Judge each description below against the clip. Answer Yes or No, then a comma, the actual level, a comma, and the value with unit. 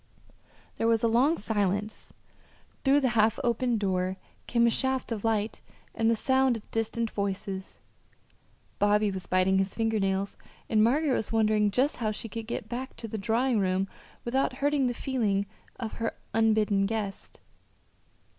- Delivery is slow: No, average, 160 wpm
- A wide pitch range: No, average, 2.8 semitones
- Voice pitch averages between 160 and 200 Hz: No, high, 225 Hz